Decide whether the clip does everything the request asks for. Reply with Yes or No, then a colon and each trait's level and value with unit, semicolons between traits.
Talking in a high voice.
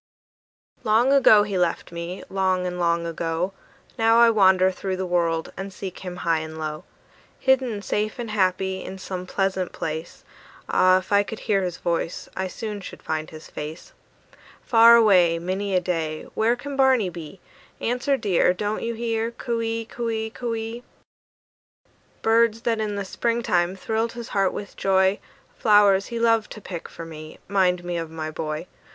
Yes: high, 195 Hz